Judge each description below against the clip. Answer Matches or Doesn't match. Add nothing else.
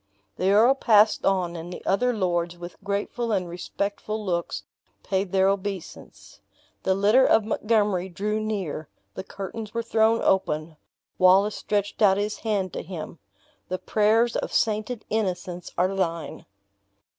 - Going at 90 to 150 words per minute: Matches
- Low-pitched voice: Doesn't match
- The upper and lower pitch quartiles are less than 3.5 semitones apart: Matches